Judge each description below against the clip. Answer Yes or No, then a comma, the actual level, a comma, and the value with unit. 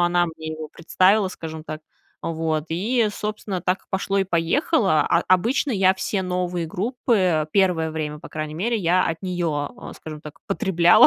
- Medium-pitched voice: Yes, medium, 175 Hz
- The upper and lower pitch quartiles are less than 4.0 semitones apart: Yes, average, 3.4 semitones